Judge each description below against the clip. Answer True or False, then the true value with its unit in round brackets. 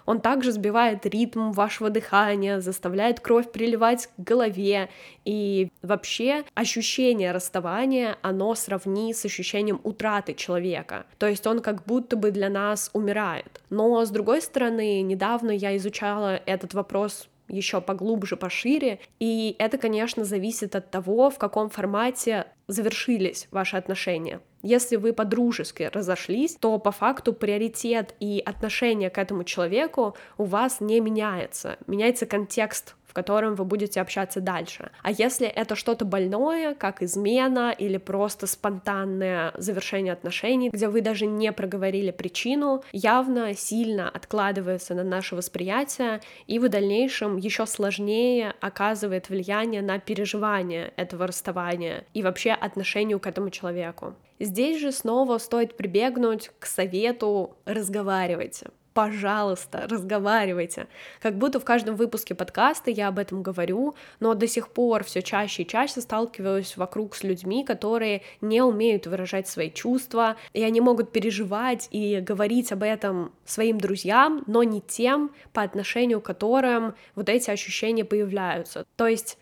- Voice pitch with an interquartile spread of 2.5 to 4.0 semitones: True (2.9 semitones)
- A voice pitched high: True (210 Hz)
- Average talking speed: True (135 wpm)